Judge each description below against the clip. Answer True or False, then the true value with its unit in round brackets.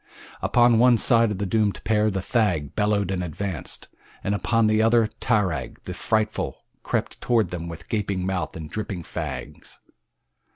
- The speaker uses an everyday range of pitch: True (3.4 semitones)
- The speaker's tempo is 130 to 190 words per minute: True (160 wpm)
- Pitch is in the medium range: False (105 Hz)